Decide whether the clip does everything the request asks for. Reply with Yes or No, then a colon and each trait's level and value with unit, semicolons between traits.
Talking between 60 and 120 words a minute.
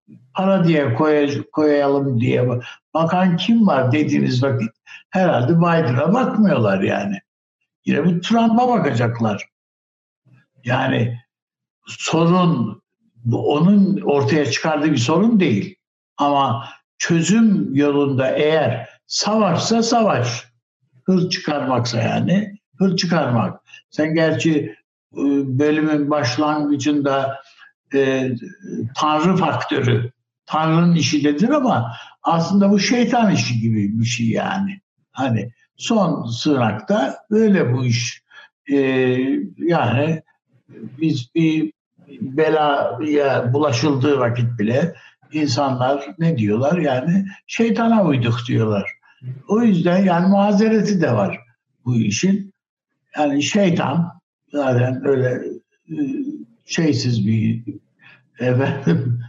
Yes: slow, 95 wpm